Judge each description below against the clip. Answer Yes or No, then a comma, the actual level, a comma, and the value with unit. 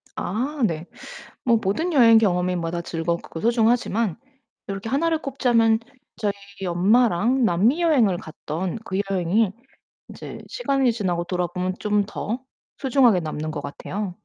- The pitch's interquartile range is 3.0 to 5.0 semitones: No, wide, 5.4 semitones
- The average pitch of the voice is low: No, high, 210 Hz